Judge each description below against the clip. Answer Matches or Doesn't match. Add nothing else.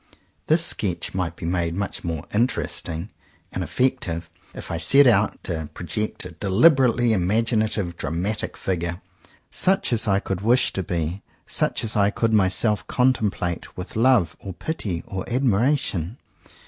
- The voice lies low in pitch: Matches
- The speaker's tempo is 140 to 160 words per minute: Matches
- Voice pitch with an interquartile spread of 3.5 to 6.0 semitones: Matches